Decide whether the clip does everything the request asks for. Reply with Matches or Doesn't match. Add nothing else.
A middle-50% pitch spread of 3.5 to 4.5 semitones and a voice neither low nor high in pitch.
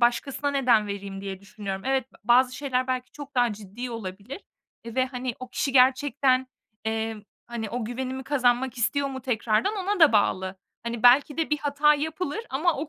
Doesn't match